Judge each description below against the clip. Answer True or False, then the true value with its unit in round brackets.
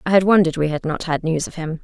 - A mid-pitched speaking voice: True (165 Hz)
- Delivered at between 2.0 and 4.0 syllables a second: False (7.0 syllables/s)